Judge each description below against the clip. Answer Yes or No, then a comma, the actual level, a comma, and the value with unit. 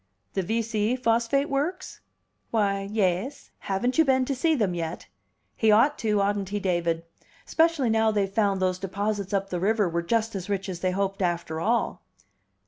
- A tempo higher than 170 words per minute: Yes, average, 180 wpm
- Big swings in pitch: No, average, 3.5 semitones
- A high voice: Yes, high, 205 Hz